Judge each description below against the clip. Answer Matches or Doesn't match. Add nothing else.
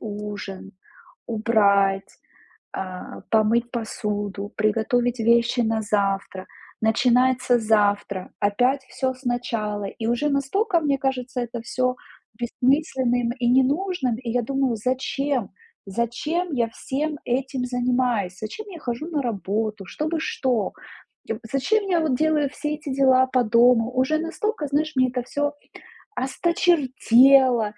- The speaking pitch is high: Matches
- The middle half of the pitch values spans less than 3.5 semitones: Doesn't match